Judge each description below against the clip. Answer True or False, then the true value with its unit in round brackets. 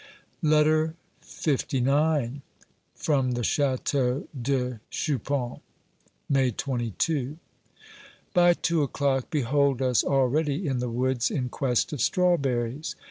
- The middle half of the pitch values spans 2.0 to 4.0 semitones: True (3.3 semitones)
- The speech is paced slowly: True (100 wpm)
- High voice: False (135 Hz)